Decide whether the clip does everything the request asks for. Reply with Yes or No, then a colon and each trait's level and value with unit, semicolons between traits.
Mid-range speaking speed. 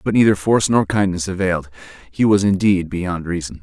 Yes: average, 180 wpm